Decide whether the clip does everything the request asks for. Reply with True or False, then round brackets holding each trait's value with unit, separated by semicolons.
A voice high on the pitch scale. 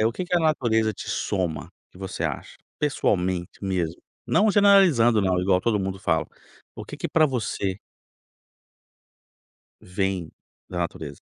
False (95 Hz)